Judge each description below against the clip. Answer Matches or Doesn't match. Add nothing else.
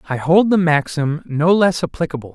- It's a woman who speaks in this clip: Doesn't match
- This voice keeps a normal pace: Matches